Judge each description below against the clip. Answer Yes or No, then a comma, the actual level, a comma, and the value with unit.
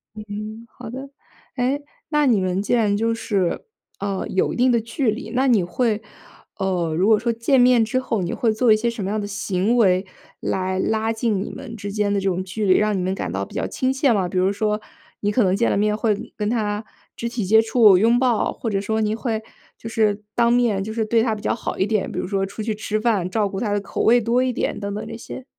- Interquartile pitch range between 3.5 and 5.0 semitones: No, average, 2.7 semitones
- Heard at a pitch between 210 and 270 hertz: Yes, high, 215 Hz